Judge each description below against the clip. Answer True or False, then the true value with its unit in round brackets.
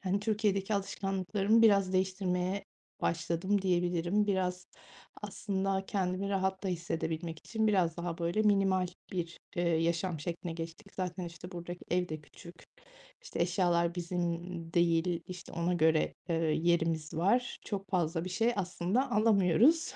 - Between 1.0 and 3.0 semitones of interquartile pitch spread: True (2.5 semitones)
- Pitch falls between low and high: True (180 Hz)